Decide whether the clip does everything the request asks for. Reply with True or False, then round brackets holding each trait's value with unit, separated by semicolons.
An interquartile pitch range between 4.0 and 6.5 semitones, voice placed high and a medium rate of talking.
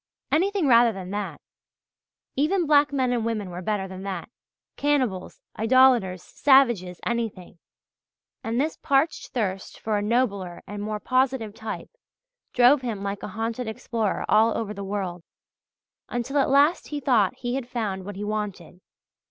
True (4.5 semitones; 225 Hz; 150 wpm)